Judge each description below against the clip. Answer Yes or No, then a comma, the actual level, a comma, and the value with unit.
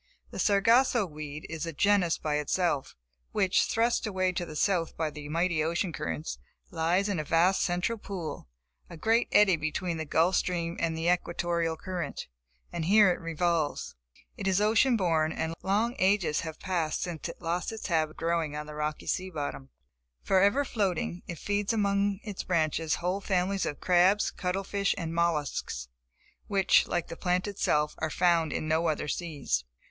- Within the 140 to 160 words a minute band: No, average, 175 wpm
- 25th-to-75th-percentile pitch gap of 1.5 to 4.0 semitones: Yes, average, 3.6 semitones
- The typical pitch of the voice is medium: Yes, medium, 175 Hz